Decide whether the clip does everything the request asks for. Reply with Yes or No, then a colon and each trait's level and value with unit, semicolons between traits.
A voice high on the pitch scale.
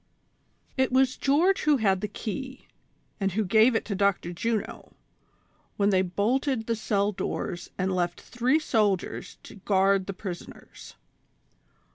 Yes: high, 210 Hz